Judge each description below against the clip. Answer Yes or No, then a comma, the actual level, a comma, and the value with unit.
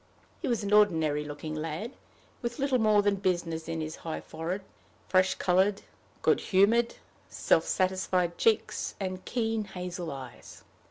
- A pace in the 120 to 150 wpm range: Yes, average, 145 wpm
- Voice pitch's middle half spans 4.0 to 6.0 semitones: Yes, average, 4.3 semitones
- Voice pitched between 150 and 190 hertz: Yes, medium, 185 Hz